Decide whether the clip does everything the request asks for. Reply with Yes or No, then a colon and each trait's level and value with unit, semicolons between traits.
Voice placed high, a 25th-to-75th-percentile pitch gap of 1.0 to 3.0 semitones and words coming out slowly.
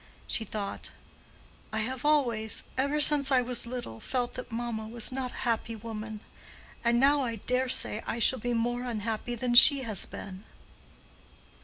No: high, 240 Hz; narrow, 2.6 semitones; average, 165 wpm